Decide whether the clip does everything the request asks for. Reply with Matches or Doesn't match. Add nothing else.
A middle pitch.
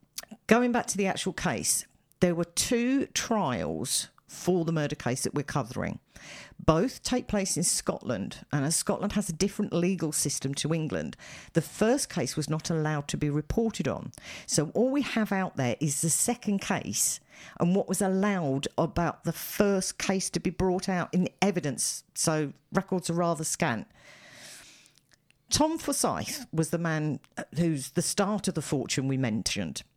Matches